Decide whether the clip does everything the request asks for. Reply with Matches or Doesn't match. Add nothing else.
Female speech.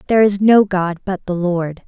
Matches